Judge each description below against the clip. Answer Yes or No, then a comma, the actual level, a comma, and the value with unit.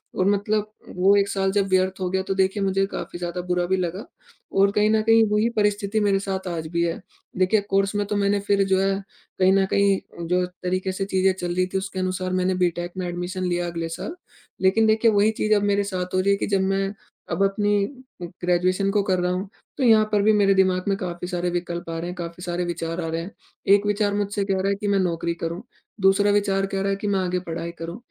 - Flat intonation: Yes, narrow, 2.0 semitones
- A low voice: No, high, 190 Hz